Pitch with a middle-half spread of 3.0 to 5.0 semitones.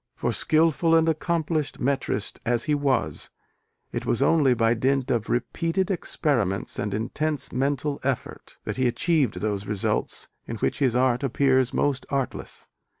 Yes: average, 4.2 semitones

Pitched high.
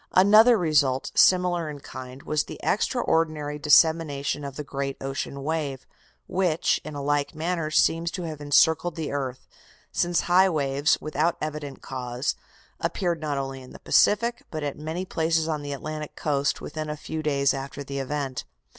No: medium, 150 Hz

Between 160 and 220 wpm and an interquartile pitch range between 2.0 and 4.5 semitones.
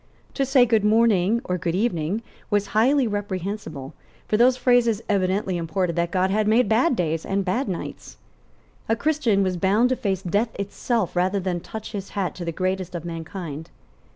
Yes: average, 180 wpm; average, 3.9 semitones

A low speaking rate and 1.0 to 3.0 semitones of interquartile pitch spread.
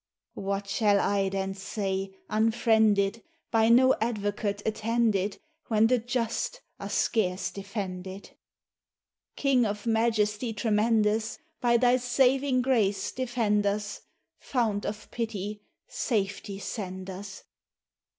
Yes: slow, 105 wpm; average, 2.7 semitones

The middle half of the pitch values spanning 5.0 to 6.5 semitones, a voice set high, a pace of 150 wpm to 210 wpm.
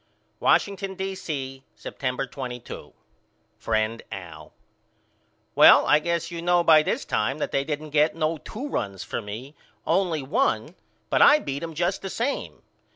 No: wide, 5.4 semitones; medium, 150 Hz; average, 155 wpm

